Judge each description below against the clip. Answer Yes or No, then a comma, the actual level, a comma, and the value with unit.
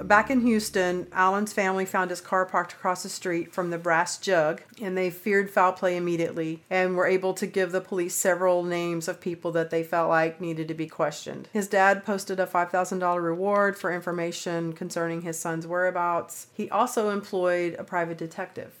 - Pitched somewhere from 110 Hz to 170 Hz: No, medium, 180 Hz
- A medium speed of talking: Yes, average, 190 wpm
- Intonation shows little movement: Yes, narrow, 2.0 semitones